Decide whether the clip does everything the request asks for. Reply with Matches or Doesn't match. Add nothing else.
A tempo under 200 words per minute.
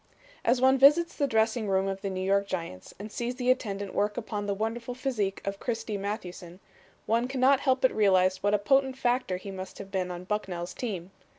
Doesn't match